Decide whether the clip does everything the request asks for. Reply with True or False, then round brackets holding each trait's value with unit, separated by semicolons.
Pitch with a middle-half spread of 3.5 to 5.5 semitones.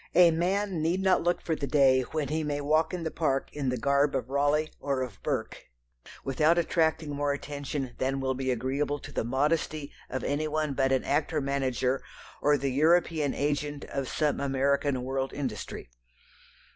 False (2.5 semitones)